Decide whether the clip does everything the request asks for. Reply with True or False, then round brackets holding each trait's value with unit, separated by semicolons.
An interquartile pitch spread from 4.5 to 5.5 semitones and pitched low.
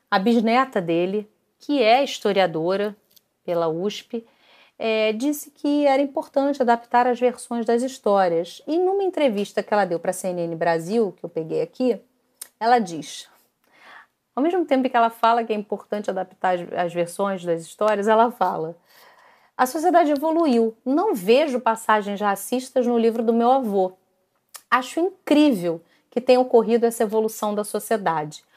False (4.8 semitones; 230 Hz)